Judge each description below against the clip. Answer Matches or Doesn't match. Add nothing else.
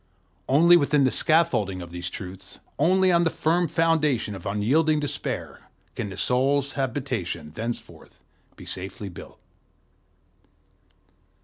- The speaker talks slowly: Matches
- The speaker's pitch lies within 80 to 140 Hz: Matches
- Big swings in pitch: Matches